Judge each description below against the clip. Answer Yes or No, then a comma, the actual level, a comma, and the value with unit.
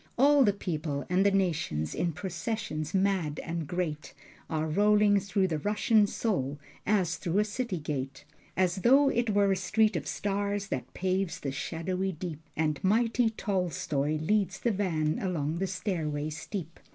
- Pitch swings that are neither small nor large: Yes, average, 4.7 semitones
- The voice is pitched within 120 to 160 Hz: No, medium, 185 Hz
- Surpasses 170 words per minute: No, average, 160 wpm